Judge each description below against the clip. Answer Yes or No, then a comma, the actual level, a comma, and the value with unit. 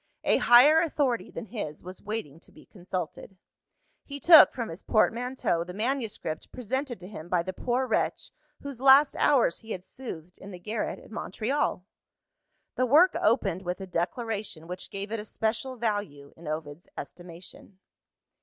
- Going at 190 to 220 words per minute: No, average, 165 wpm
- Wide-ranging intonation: Yes, wide, 5.9 semitones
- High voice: Yes, high, 215 Hz